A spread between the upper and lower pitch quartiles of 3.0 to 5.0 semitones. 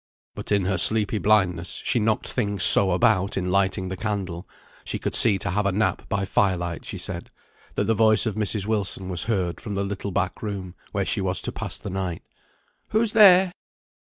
No: narrow, 2.6 semitones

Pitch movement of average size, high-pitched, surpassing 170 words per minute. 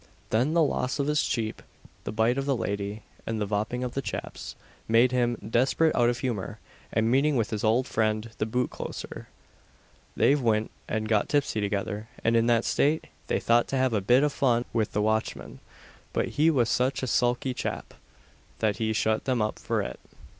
No: average, 3.1 semitones; low, 115 Hz; average, 195 wpm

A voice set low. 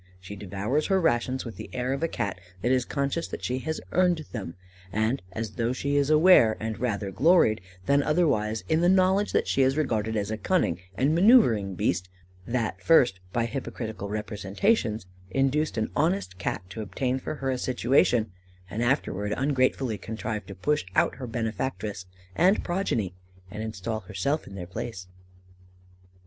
Yes: low, 120 Hz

